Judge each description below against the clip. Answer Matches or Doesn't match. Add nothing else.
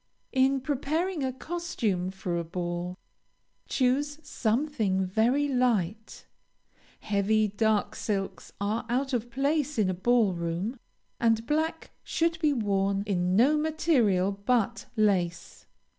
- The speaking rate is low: Matches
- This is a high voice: Matches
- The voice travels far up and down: Matches